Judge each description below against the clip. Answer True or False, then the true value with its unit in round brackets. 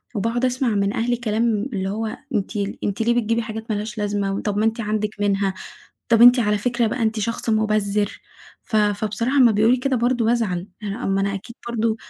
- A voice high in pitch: True (220 Hz)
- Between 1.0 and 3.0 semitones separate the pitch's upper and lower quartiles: True (2.4 semitones)